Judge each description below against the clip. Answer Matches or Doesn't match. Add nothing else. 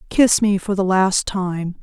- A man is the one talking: Doesn't match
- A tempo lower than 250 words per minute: Matches